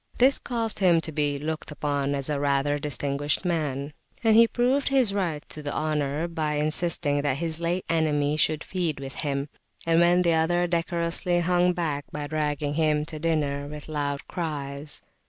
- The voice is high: No, medium, 155 Hz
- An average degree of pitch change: Yes, average, 3.0 semitones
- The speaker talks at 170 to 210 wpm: Yes, average, 175 wpm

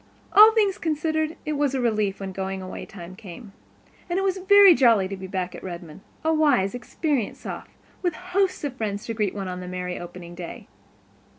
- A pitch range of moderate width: No, wide, 9.0 semitones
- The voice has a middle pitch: No, high, 225 Hz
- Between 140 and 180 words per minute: No, average, 195 wpm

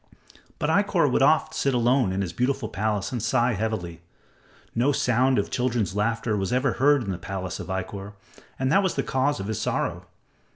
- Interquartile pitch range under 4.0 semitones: No, average, 4.8 semitones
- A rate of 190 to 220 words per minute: Yes, average, 195 wpm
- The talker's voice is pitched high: No, low, 115 Hz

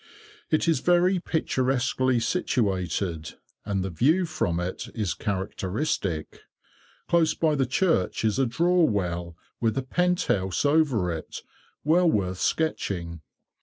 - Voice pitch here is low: Yes, low, 120 Hz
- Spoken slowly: Yes, slow, 130 wpm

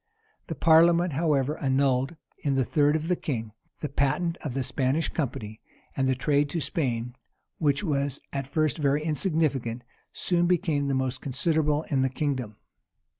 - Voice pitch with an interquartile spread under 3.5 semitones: Yes, average, 3.1 semitones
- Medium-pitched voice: Yes, medium, 145 Hz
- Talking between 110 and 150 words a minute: No, average, 160 wpm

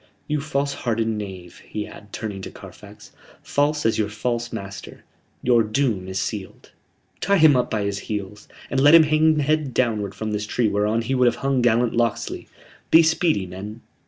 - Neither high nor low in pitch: No, low, 115 Hz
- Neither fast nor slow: Yes, average, 185 wpm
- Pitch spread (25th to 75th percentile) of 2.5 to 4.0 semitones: No, average, 5.1 semitones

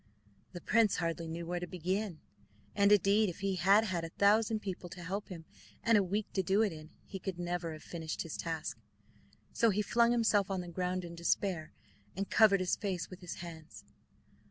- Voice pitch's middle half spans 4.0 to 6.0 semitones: No, average, 3.0 semitones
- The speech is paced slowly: No, fast, 205 wpm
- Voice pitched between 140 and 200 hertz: Yes, medium, 185 Hz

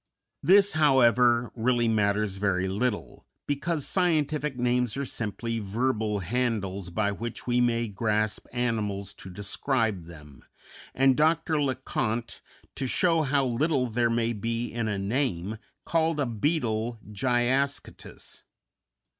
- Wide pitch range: No, average, 4.1 semitones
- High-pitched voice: No, low, 120 Hz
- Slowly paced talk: Yes, slow, 125 wpm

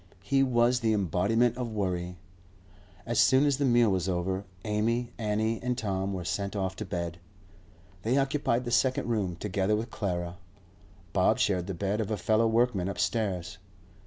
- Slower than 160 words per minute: No, average, 165 wpm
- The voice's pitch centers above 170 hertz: No, low, 105 Hz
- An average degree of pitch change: Yes, average, 4.0 semitones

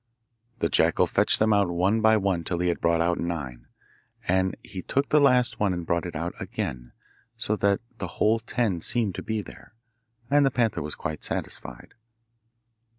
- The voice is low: Yes, very low, 95 Hz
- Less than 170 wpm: No, average, 180 wpm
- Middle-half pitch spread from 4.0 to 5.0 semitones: Yes, average, 4.6 semitones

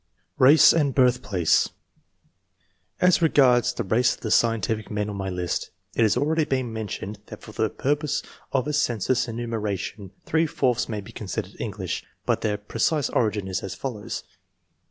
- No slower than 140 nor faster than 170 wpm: Yes, average, 160 wpm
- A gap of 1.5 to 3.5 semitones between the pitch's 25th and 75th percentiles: No, average, 4.1 semitones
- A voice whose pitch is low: Yes, low, 115 Hz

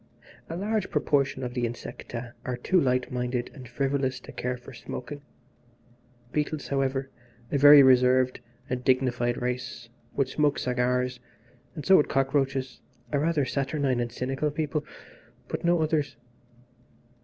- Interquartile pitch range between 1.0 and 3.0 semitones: Yes, narrow, 2.6 semitones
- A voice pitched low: Yes, low, 130 Hz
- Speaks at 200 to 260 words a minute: No, average, 140 wpm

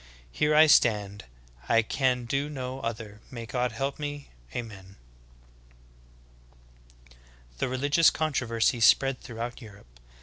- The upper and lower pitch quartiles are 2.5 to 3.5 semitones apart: No, average, 3.9 semitones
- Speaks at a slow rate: Yes, slow, 115 wpm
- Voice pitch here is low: Yes, low, 120 Hz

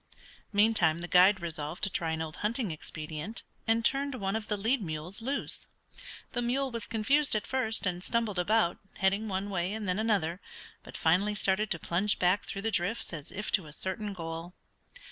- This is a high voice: Yes, high, 200 Hz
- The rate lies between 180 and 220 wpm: Yes, average, 190 wpm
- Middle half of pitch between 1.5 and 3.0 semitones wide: No, average, 4.3 semitones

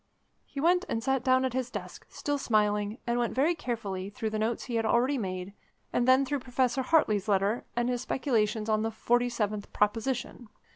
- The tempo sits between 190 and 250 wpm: Yes, average, 195 wpm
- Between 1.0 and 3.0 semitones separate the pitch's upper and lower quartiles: No, average, 3.4 semitones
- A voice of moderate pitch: No, high, 235 Hz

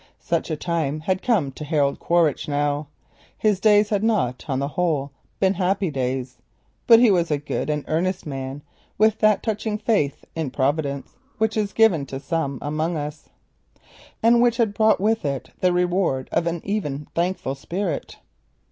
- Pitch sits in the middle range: Yes, medium, 165 Hz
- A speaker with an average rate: Yes, average, 170 wpm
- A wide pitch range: Yes, wide, 6.1 semitones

